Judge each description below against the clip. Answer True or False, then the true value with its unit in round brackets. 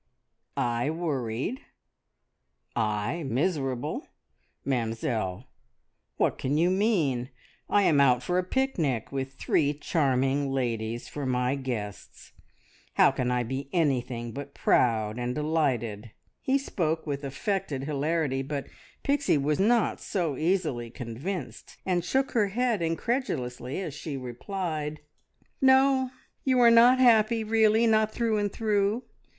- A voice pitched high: False (150 Hz)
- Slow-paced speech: True (125 wpm)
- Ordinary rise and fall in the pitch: False (8.2 semitones)